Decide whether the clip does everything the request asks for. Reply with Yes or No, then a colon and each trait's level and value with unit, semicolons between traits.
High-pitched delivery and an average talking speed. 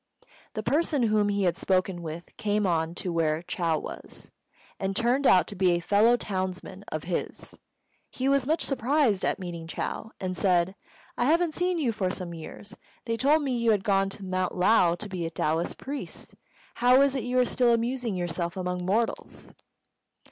Yes: high, 200 Hz; average, 185 wpm